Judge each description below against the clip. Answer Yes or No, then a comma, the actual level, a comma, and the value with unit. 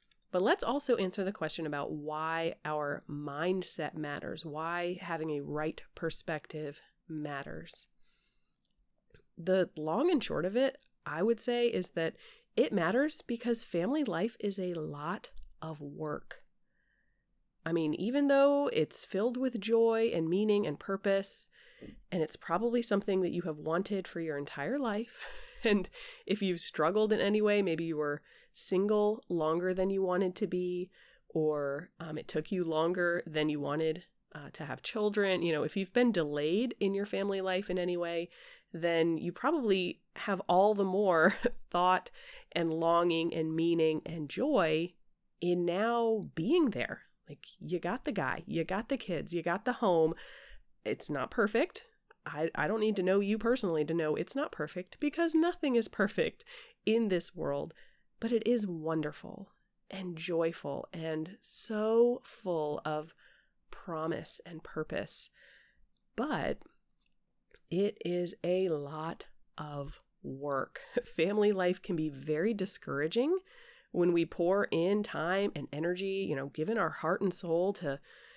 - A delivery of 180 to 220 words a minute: No, average, 155 wpm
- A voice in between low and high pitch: Yes, medium, 180 Hz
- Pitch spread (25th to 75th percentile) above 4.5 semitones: Yes, average, 5.0 semitones